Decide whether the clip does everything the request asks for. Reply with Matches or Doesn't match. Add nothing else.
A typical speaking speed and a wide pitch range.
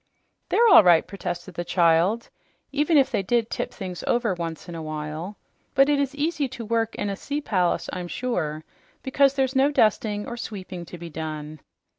Matches